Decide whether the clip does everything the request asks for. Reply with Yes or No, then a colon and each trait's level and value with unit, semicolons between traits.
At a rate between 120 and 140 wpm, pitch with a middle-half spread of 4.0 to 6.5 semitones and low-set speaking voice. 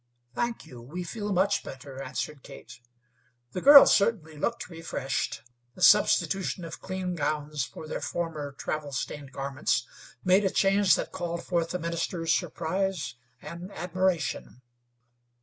No: slow, 135 wpm; average, 4.5 semitones; medium, 170 Hz